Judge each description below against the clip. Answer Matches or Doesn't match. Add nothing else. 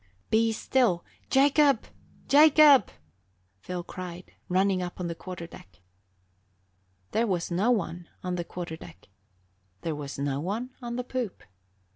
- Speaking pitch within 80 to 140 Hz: Doesn't match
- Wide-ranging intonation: Matches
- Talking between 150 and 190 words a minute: Doesn't match